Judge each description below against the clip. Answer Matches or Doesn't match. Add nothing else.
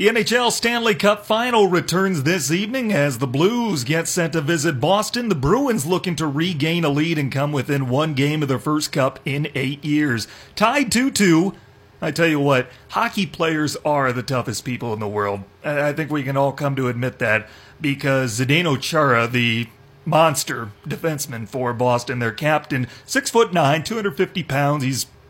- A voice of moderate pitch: Matches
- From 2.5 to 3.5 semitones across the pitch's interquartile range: Doesn't match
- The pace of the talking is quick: Doesn't match